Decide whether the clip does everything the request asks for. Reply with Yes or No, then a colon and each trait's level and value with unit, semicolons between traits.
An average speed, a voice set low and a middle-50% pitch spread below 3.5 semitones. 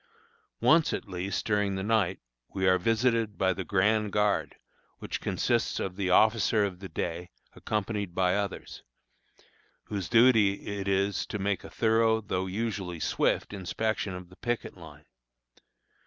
Yes: average, 150 wpm; low, 100 Hz; average, 2.8 semitones